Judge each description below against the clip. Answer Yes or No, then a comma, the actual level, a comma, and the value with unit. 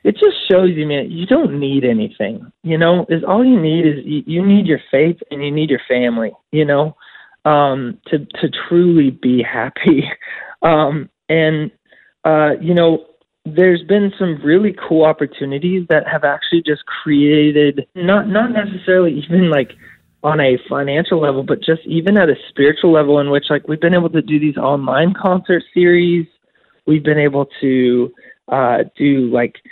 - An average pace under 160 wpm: No, average, 175 wpm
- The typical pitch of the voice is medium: Yes, medium, 155 Hz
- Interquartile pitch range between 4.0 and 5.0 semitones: No, average, 3.4 semitones